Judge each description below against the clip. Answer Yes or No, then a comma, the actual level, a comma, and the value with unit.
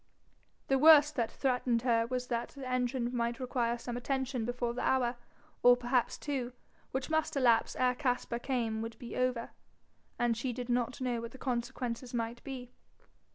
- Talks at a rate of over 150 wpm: Yes, average, 170 wpm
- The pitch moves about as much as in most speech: No, narrow, 1.6 semitones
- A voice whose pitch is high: Yes, high, 245 Hz